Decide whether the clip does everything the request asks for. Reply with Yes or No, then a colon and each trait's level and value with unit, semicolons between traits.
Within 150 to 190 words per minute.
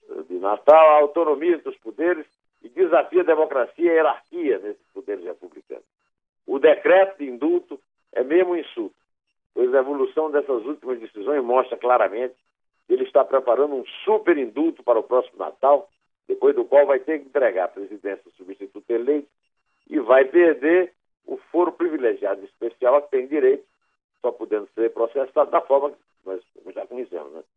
Yes: average, 170 wpm